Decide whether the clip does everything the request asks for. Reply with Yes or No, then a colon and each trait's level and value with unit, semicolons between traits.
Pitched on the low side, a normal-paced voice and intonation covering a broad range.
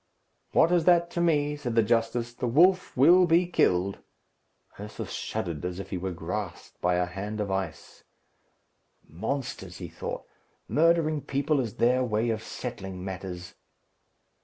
Yes: low, 115 Hz; average, 150 wpm; wide, 7.7 semitones